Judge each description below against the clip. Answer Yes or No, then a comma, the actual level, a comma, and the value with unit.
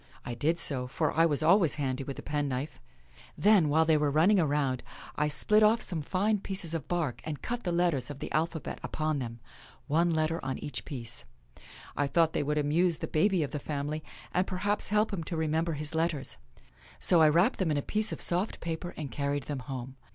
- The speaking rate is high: Yes, fast, 215 wpm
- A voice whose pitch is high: No, medium, 155 Hz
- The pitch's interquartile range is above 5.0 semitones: No, average, 3.4 semitones